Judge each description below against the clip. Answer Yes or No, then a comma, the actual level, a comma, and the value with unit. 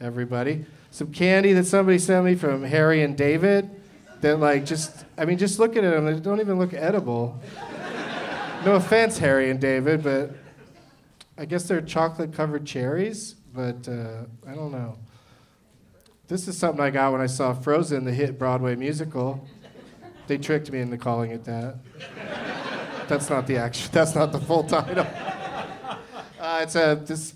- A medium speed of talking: Yes, average, 160 wpm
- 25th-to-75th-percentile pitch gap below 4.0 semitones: No, average, 4.8 semitones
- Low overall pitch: No, medium, 150 Hz